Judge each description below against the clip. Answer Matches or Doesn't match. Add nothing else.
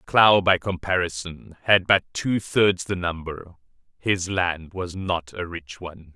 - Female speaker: Doesn't match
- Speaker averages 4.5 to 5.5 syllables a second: Doesn't match